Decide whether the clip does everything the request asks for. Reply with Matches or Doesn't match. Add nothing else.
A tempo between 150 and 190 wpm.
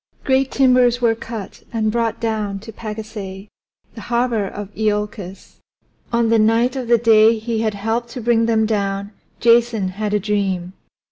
Matches